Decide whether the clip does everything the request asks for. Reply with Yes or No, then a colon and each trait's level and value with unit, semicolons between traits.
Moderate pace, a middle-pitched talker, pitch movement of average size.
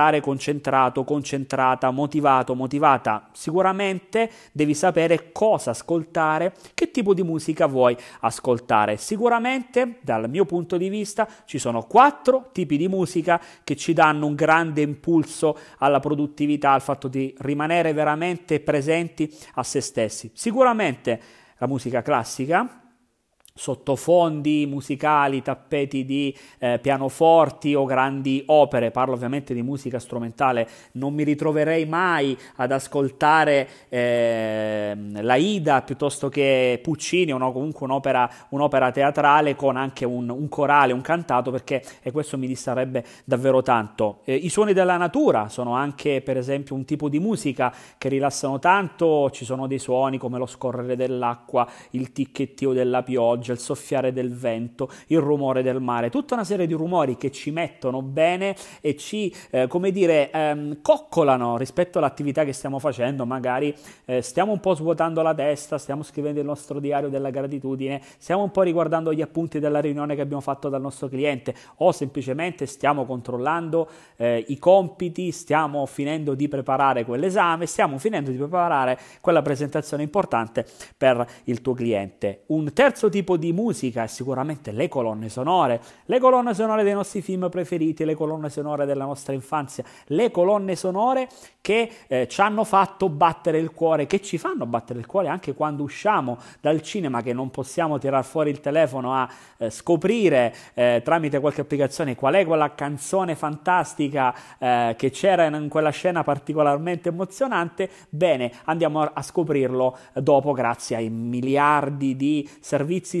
Yes: average, 150 wpm; medium, 145 Hz; average, 4.2 semitones